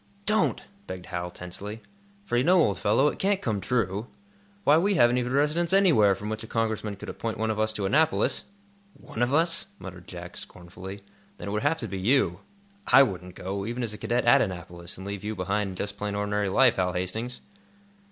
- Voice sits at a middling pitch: No, low, 105 Hz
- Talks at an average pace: No, fast, 210 wpm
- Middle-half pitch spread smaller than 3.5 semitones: No, average, 4.7 semitones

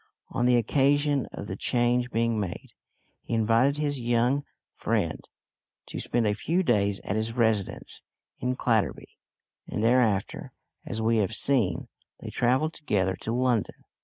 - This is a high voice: No, low, 120 Hz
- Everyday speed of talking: Yes, average, 145 wpm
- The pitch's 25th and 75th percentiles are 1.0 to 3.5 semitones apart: Yes, average, 2.8 semitones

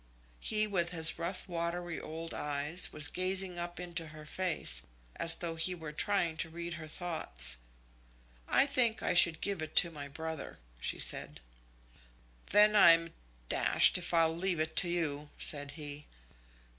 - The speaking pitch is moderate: Yes, medium, 170 Hz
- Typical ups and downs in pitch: No, narrow, 2.3 semitones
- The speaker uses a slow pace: No, average, 155 wpm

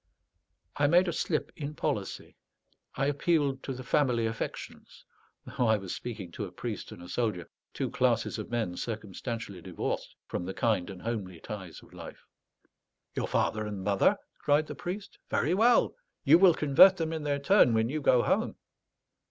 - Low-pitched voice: Yes, low, 120 Hz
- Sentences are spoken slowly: No, average, 175 wpm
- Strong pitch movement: Yes, wide, 6.2 semitones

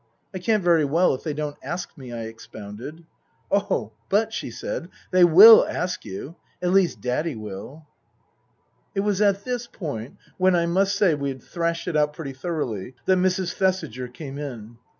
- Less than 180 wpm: No, average, 190 wpm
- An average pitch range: No, wide, 6.1 semitones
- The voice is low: No, medium, 165 Hz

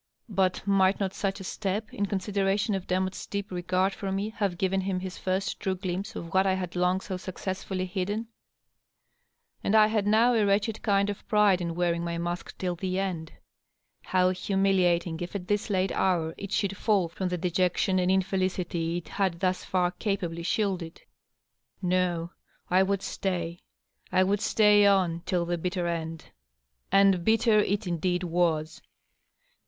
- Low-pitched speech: No, medium, 185 Hz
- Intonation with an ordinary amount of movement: No, narrow, 2.0 semitones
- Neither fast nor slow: Yes, average, 170 wpm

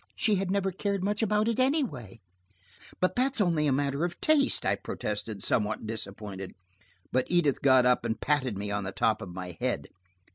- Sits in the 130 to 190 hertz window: Yes, medium, 140 Hz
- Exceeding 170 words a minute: Yes, average, 185 wpm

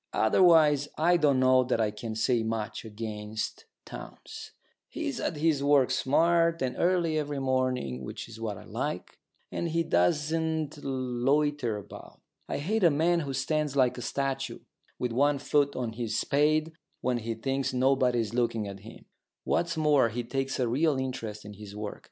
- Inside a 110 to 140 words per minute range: No, average, 170 wpm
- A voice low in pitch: Yes, low, 130 Hz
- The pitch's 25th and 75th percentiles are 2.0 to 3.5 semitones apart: No, average, 4.7 semitones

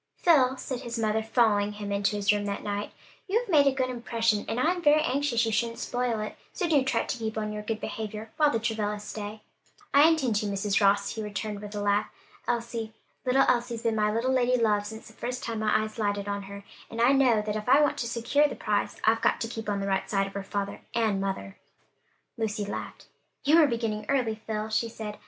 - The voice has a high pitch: Yes, high, 220 Hz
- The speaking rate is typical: No, fast, 235 wpm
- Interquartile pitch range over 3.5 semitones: No, average, 2.9 semitones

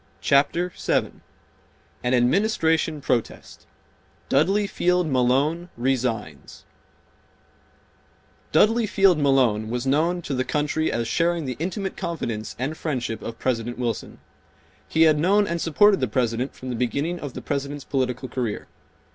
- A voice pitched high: No, medium, 140 Hz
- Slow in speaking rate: Yes, slow, 130 wpm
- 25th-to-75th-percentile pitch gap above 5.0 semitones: Yes, wide, 5.4 semitones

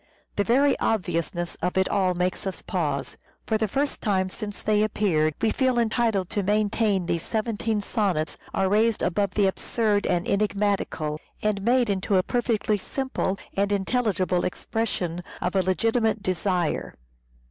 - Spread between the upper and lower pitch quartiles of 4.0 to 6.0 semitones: No, average, 3.1 semitones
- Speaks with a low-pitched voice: No, high, 200 Hz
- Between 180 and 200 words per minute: No, average, 150 wpm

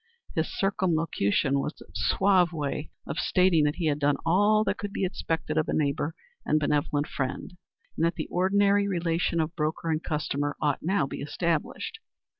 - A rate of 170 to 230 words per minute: Yes, average, 175 wpm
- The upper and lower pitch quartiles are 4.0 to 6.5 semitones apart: No, average, 3.6 semitones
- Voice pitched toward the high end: No, medium, 160 Hz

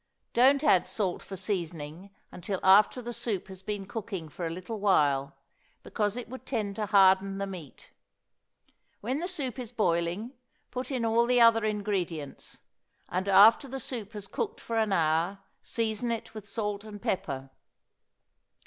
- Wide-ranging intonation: No, average, 3.8 semitones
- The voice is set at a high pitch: Yes, high, 205 Hz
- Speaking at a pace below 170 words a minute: Yes, average, 160 wpm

